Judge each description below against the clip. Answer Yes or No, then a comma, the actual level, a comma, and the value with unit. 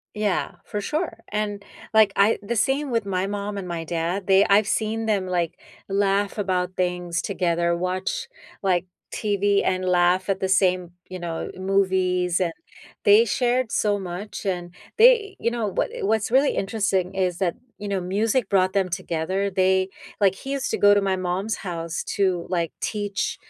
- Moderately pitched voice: No, high, 195 Hz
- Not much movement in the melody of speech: Yes, narrow, 2.3 semitones